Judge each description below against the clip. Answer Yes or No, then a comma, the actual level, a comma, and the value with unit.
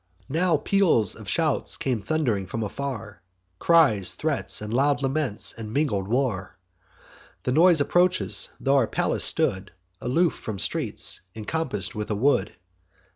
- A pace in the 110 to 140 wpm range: Yes, slow, 135 wpm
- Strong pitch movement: Yes, wide, 6.6 semitones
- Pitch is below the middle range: Yes, low, 130 Hz